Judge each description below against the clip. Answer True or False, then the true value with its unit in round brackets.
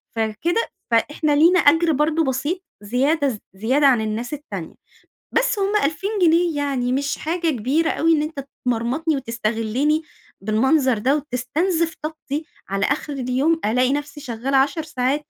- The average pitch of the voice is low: False (285 Hz)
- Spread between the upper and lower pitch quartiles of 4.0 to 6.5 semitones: True (4.3 semitones)